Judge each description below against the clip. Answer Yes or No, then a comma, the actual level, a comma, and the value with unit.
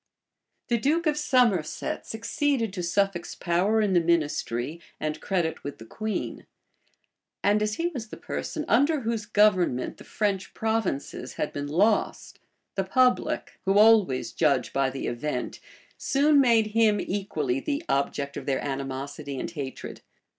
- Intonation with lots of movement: Yes, wide, 7.6 semitones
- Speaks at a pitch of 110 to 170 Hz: No, high, 195 Hz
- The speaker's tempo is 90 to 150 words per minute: Yes, average, 145 wpm